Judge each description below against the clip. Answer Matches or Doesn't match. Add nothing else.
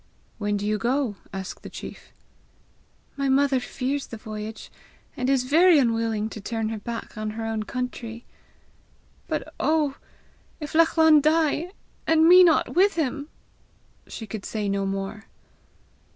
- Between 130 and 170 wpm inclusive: Matches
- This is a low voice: Doesn't match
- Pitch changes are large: Matches